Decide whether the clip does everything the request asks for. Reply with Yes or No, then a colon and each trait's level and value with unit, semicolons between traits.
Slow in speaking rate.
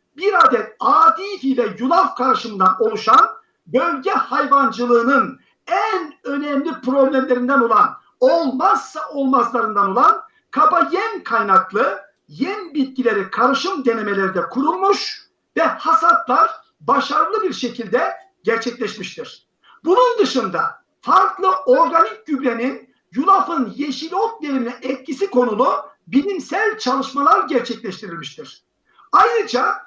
Yes: slow, 90 wpm